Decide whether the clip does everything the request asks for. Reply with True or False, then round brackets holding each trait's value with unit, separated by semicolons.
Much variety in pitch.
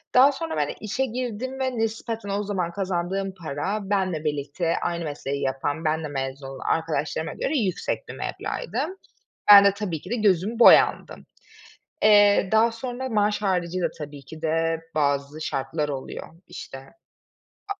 True (5.9 semitones)